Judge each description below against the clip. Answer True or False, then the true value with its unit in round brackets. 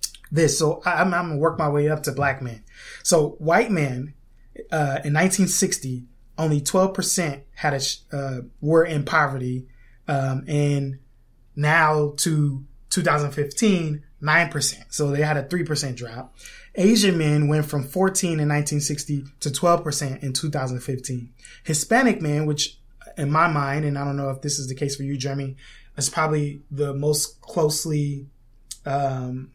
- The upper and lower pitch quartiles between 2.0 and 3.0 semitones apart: True (2.4 semitones)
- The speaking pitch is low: False (145 Hz)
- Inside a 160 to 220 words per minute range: False (150 wpm)